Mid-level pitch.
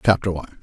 No: very low, 90 Hz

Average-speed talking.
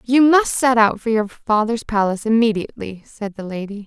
Yes: average, 185 wpm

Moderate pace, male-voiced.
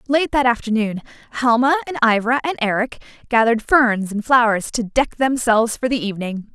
No: average, 165 wpm; female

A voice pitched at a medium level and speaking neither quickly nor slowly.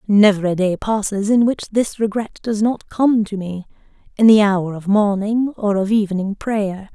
No: high, 205 Hz; average, 190 wpm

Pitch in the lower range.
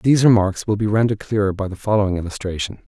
Yes: low, 100 Hz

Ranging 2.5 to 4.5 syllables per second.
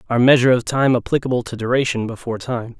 No: 6.8 syllables/s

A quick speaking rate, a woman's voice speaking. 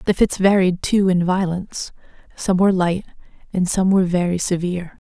No: average, 165 wpm; female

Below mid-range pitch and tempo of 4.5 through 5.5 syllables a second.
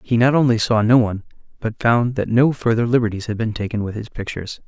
No: low, 115 Hz; 6.3 syllables/s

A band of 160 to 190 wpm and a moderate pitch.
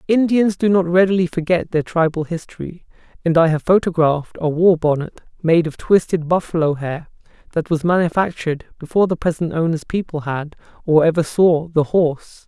Yes: average, 165 wpm; medium, 165 Hz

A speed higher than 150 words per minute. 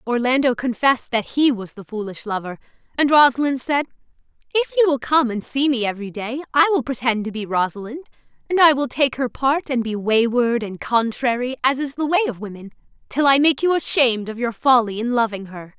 Yes: average, 200 wpm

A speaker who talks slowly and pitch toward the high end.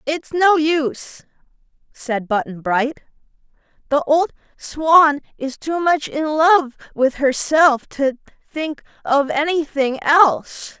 Yes: slow, 115 wpm; very high, 290 Hz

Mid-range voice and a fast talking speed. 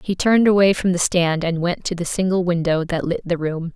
Yes: medium, 175 Hz; fast, 255 wpm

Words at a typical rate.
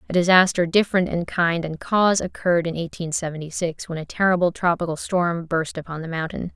Yes: average, 190 wpm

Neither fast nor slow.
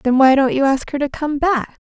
No: fast, 290 wpm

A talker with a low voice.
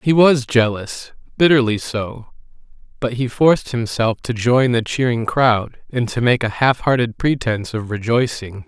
Yes: low, 120 Hz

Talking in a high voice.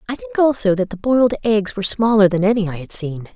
Yes: high, 200 Hz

